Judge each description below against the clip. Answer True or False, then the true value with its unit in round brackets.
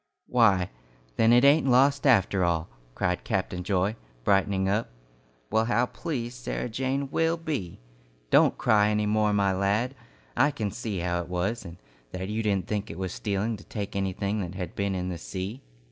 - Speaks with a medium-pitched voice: False (105 Hz)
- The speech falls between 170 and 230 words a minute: True (180 wpm)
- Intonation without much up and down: False (4.1 semitones)